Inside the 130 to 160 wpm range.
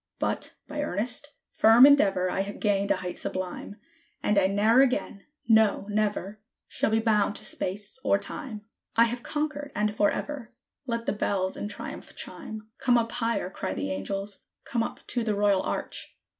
No: average, 170 wpm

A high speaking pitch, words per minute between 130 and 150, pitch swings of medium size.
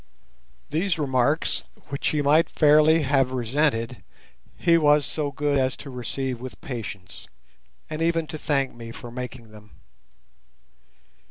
No: medium, 140 Hz; slow, 135 wpm; average, 3.7 semitones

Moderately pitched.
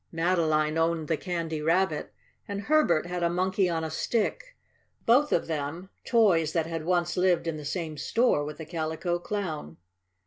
Yes: medium, 170 Hz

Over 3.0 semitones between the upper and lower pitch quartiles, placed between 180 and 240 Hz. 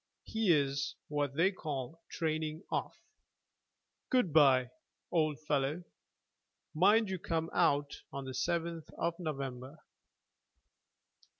No: average, 3.4 semitones; medium, 155 Hz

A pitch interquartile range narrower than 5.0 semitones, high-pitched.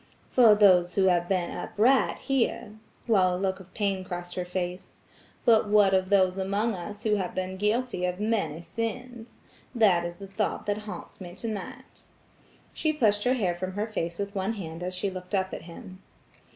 Yes: average, 2.8 semitones; high, 195 Hz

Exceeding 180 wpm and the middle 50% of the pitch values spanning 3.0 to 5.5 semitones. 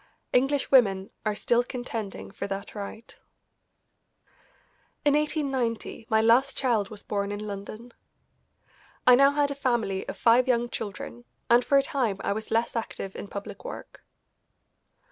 No: average, 145 wpm; average, 4.2 semitones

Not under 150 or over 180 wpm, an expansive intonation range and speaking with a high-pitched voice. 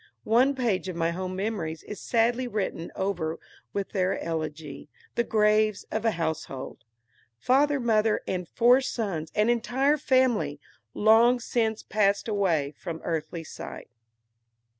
No: slow, 135 wpm; wide, 6.0 semitones; high, 210 Hz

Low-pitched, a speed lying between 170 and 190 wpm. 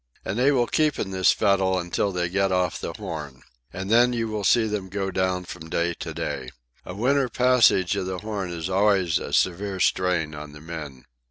No: very low, 95 Hz; fast, 205 wpm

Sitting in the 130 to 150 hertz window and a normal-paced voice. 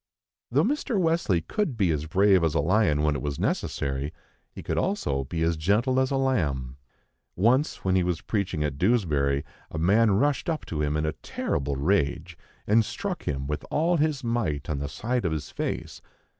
No: very low, 90 Hz; average, 195 wpm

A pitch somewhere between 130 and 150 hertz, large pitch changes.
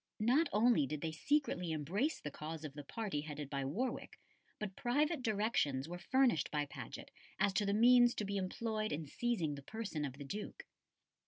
No: high, 195 Hz; wide, 7.8 semitones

